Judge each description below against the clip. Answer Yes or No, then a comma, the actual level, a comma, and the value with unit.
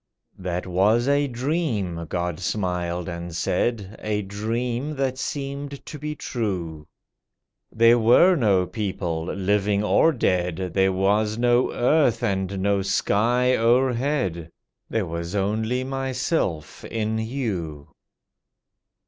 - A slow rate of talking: Yes, slow, 110 wpm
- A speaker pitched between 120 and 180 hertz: No, low, 105 Hz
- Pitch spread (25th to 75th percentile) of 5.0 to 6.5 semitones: Yes, wide, 5.5 semitones